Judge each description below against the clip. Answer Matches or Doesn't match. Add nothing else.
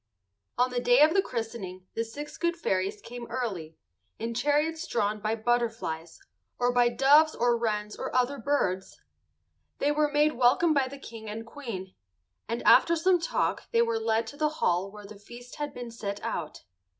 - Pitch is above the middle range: Matches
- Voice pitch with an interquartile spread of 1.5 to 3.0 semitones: Doesn't match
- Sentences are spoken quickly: Doesn't match